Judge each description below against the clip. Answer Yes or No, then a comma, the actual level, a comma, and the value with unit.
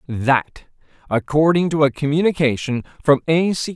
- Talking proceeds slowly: Yes, slow, 130 wpm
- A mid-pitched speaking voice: Yes, medium, 150 Hz